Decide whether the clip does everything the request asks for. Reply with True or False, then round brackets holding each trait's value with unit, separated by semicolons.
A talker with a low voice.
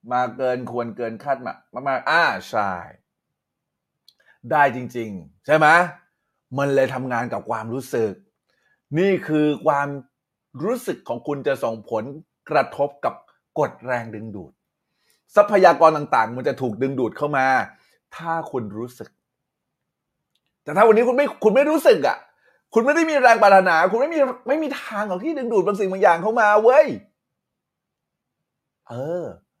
False (150 Hz)